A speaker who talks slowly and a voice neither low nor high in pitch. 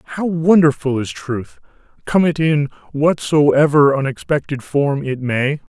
Yes: slow, 125 wpm; medium, 145 Hz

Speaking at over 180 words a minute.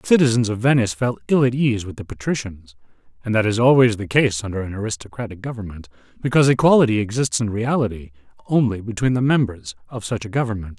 Yes: average, 190 wpm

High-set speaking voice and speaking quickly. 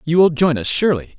No: medium, 155 Hz; fast, 255 wpm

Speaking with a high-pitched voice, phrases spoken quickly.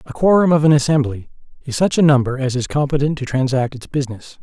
No: medium, 140 Hz; fast, 215 wpm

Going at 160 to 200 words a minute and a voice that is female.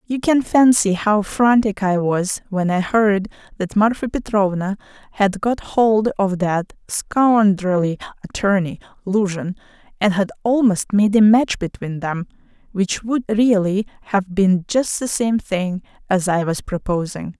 No: average, 140 wpm; female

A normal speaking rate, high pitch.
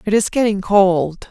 Yes: average, 185 wpm; high, 195 Hz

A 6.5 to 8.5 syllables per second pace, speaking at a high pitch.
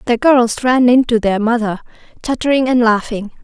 No: 5.2 syllables/s; high, 235 Hz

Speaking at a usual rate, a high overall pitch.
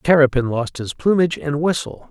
No: average, 170 wpm; medium, 145 Hz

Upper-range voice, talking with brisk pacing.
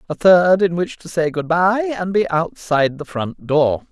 No: medium, 170 Hz; fast, 215 wpm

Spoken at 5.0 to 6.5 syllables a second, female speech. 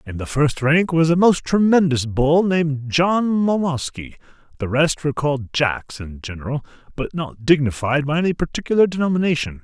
No: 5.2 syllables/s; male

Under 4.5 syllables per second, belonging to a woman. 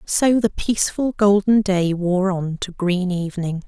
Yes: 4.2 syllables/s; female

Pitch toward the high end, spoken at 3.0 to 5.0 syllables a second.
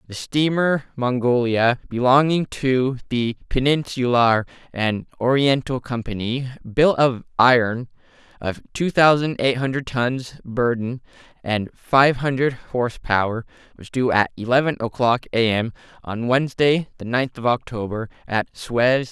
No: low, 125 Hz; 4.2 syllables/s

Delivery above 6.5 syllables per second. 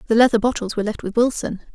Yes: 7.6 syllables/s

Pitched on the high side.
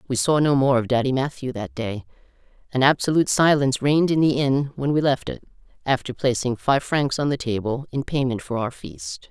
No: low, 135 Hz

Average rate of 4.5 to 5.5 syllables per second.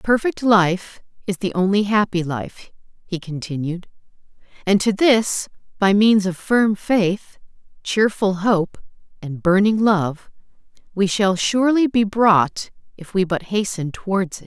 No: 4.0 syllables/s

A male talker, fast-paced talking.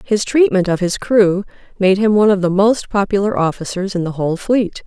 No: female; fast, 210 wpm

